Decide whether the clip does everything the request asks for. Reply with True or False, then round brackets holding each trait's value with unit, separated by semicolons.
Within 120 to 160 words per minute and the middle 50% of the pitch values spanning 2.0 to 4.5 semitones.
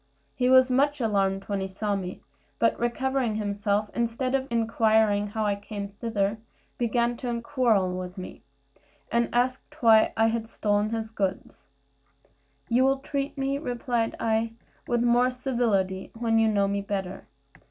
True (150 wpm; 3.2 semitones)